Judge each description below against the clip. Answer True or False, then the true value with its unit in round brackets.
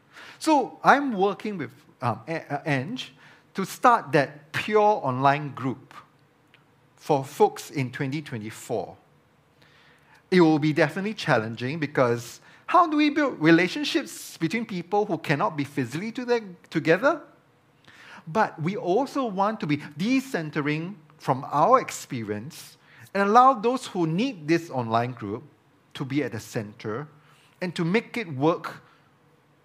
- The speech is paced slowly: True (130 wpm)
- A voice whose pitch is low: False (155 Hz)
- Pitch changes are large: True (6.1 semitones)